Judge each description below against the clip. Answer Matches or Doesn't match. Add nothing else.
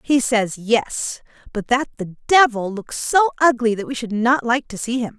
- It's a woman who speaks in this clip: Matches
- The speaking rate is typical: Doesn't match